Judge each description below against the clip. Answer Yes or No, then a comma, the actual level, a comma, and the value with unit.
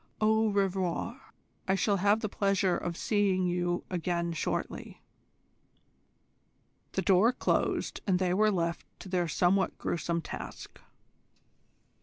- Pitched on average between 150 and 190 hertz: Yes, medium, 185 Hz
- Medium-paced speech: No, slow, 120 wpm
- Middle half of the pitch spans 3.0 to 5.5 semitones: No, narrow, 2.6 semitones